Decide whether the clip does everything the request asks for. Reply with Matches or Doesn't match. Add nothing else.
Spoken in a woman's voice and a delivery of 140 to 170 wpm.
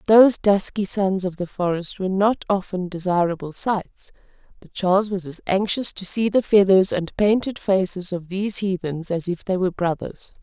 Doesn't match